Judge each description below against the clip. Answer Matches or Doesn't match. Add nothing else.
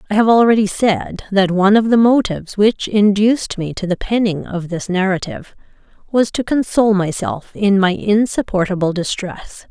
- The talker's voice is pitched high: Matches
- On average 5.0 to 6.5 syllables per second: Matches